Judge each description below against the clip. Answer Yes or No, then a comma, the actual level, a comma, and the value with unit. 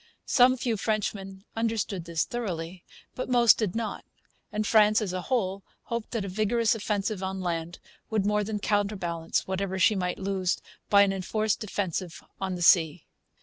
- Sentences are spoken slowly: No, average, 165 wpm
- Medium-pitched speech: No, high, 200 Hz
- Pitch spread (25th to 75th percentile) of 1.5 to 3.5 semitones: Yes, average, 2.8 semitones